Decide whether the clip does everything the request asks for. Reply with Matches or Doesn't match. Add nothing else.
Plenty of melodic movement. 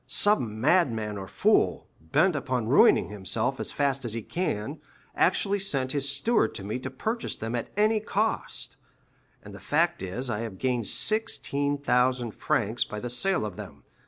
Matches